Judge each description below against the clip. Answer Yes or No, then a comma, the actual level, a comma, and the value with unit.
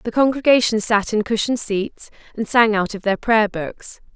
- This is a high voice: Yes, high, 220 Hz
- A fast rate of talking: No, average, 190 wpm